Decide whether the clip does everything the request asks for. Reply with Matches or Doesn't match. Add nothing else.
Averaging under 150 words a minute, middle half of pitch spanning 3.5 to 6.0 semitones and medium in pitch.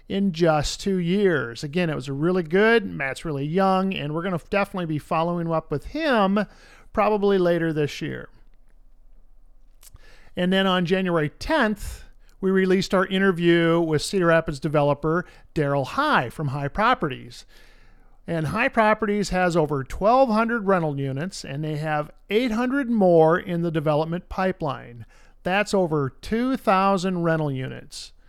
Matches